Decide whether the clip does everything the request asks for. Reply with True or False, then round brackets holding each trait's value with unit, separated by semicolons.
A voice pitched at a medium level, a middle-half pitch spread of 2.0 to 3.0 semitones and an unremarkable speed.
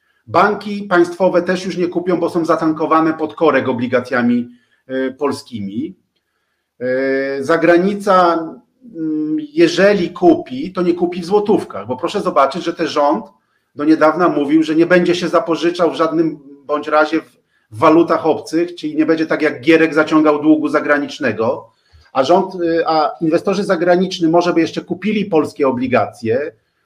True (165 Hz; 2.6 semitones; 150 wpm)